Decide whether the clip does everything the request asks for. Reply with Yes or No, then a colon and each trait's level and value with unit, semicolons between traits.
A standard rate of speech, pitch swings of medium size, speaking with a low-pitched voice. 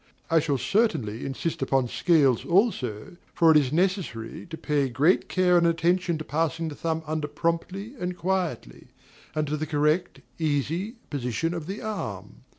No: average, 160 wpm; average, 3.6 semitones; medium, 160 Hz